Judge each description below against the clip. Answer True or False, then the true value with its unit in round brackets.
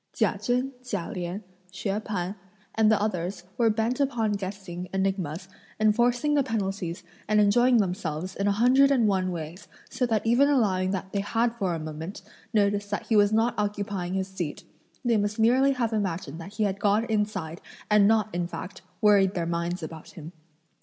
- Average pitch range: True (3.3 semitones)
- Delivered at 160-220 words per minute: True (180 wpm)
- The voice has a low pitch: False (205 Hz)